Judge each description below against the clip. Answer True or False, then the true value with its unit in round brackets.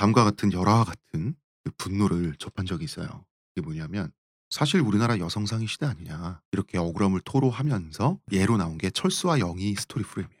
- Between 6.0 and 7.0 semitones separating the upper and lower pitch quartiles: True (6.6 semitones)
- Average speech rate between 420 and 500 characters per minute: False (410 characters per minute)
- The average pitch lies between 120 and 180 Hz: False (105 Hz)